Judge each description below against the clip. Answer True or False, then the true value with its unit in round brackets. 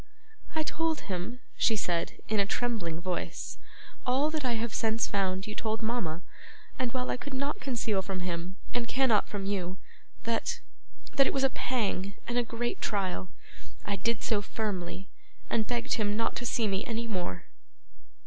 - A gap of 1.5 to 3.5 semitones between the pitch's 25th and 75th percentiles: False (4.2 semitones)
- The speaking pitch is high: True (220 Hz)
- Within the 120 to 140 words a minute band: False (175 wpm)